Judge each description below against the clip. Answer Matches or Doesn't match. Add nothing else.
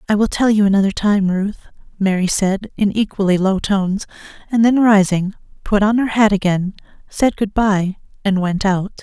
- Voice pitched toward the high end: Matches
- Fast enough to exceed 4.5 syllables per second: Matches